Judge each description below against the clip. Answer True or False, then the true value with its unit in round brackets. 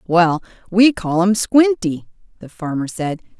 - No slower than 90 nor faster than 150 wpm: True (140 wpm)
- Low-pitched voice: False (190 Hz)